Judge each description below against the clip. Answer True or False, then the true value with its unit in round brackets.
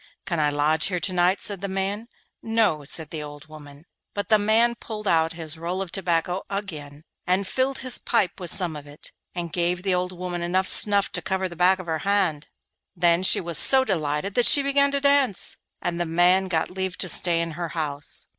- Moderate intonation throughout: True (3.6 semitones)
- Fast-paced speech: True (215 wpm)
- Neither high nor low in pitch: True (180 Hz)